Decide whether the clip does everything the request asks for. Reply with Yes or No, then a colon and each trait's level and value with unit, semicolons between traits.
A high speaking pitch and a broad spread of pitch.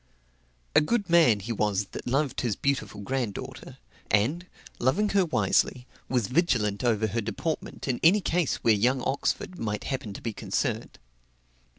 No: low, 125 Hz; wide, 6.7 semitones